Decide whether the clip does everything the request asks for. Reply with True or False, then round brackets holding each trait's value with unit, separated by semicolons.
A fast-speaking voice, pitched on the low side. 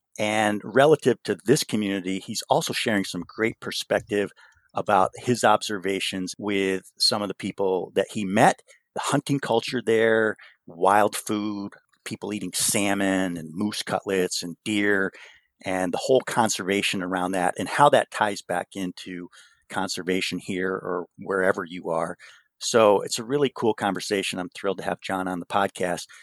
False (155 wpm; 100 Hz)